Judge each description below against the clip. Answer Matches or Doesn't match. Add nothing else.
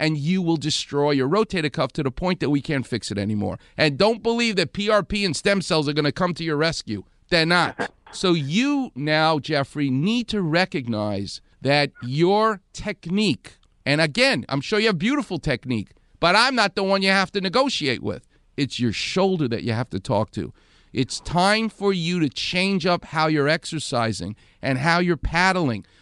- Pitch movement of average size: Doesn't match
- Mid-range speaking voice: Matches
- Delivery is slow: Doesn't match